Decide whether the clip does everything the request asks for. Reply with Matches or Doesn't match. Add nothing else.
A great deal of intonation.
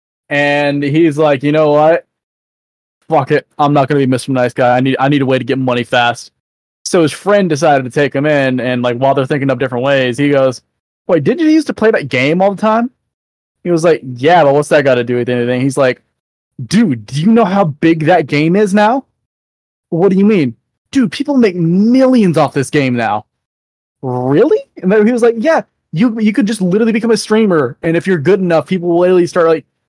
Matches